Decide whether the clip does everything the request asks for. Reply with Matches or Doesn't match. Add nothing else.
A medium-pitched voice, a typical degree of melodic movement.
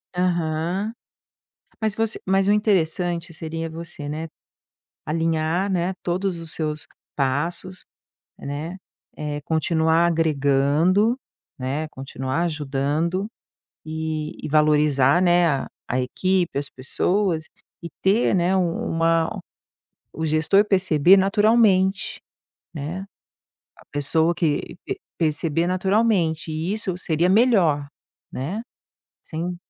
Matches